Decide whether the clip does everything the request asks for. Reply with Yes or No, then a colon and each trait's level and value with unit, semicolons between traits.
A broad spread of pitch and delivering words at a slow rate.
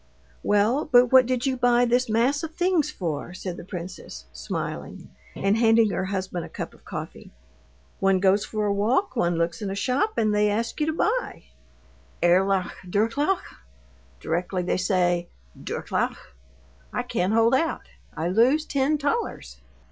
No: wide, 6.1 semitones; average, 160 wpm